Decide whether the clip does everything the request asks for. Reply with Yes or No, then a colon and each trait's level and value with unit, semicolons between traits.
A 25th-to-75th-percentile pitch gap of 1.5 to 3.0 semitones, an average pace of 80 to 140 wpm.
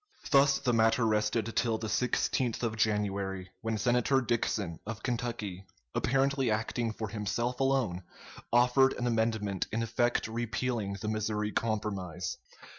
Yes: narrow, 2.4 semitones; slow, 135 wpm